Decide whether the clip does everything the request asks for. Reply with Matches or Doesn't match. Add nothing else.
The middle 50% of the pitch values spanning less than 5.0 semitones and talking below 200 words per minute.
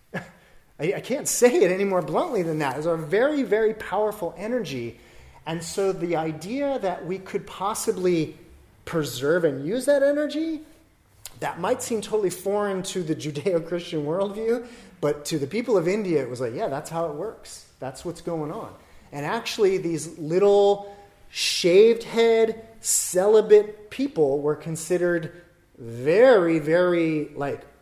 Doesn't match